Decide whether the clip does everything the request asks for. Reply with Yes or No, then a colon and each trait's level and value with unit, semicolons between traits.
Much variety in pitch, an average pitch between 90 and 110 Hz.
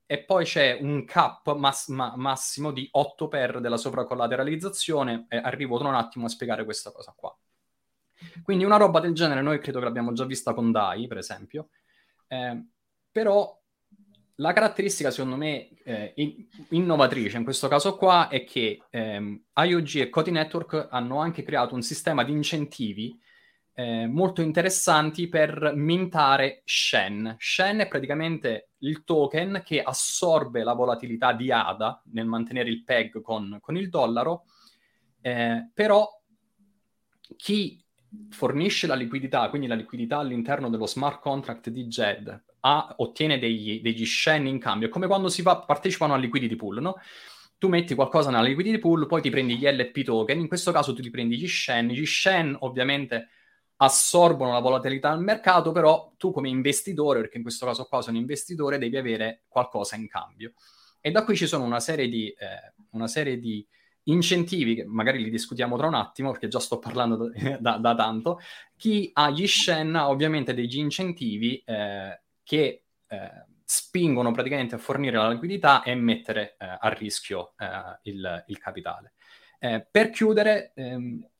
No: wide, 5.9 semitones; medium, 140 Hz